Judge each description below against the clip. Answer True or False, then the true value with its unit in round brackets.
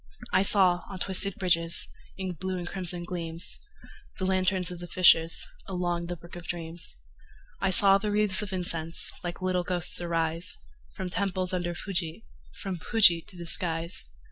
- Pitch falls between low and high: True (180 Hz)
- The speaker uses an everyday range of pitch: False (1.7 semitones)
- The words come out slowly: False (165 wpm)